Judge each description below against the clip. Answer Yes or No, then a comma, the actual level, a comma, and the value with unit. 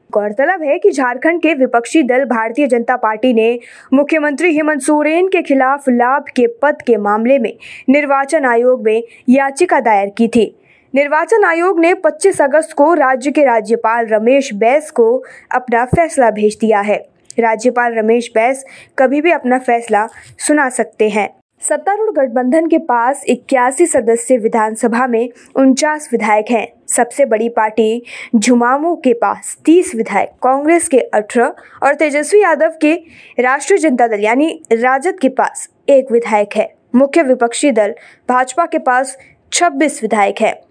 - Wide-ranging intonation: No, average, 4.7 semitones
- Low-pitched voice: No, very high, 260 Hz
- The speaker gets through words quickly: No, average, 150 wpm